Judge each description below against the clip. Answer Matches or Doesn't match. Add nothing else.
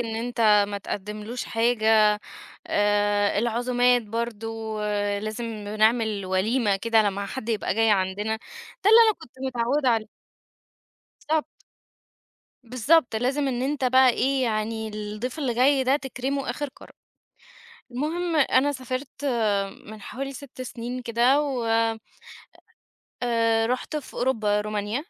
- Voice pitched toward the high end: Matches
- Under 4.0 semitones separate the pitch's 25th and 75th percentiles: Matches